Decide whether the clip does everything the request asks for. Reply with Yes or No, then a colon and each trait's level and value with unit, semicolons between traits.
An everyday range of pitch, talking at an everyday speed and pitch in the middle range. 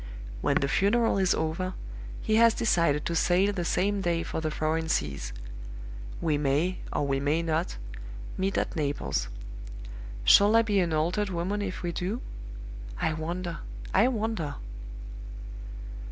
Yes: average, 4.2 semitones; average, 145 wpm; medium, 175 Hz